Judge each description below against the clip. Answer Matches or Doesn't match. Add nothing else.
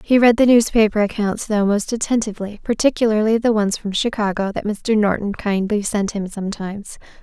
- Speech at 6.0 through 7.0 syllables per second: Doesn't match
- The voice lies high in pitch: Matches